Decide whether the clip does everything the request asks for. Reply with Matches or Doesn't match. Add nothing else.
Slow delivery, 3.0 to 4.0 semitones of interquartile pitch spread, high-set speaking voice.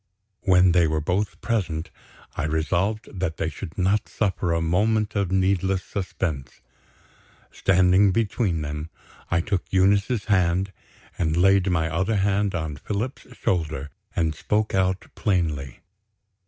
Doesn't match